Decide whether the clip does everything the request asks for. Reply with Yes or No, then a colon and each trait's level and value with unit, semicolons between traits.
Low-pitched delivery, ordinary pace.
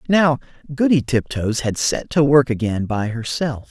Yes: low, 130 Hz; average, 160 wpm